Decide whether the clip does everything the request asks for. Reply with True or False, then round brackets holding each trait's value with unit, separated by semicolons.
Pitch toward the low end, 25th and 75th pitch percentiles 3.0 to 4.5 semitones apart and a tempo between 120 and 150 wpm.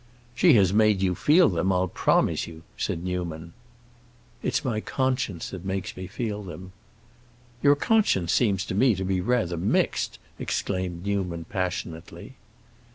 True (95 Hz; 3.5 semitones; 145 wpm)